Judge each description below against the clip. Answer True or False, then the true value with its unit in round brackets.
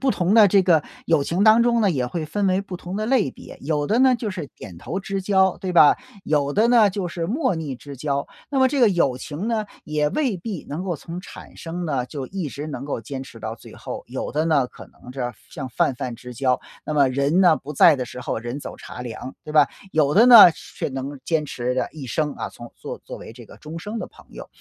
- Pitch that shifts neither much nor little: False (6.1 semitones)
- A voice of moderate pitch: True (155 Hz)